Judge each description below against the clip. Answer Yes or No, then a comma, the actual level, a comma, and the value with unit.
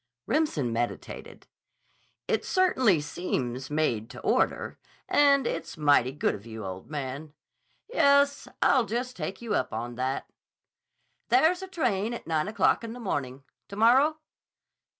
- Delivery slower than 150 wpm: Yes, average, 140 wpm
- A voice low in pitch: No, medium, 185 Hz